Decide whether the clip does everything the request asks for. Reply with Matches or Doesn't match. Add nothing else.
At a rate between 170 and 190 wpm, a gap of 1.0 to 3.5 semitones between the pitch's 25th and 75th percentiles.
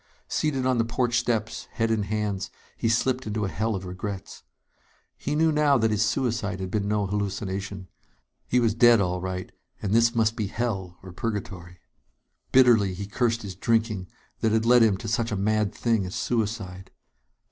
Matches